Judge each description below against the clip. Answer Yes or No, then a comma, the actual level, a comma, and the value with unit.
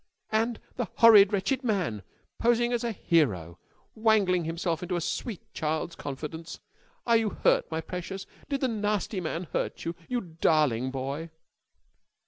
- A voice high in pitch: No, medium, 180 Hz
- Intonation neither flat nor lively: No, wide, 5.8 semitones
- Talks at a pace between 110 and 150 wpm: Yes, average, 145 wpm